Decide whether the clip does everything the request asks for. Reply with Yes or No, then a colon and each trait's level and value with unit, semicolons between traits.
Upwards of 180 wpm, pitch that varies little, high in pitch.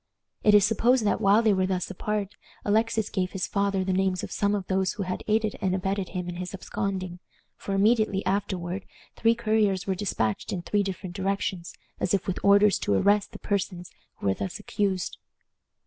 Yes: average, 195 wpm; narrow, 1.9 semitones; high, 195 Hz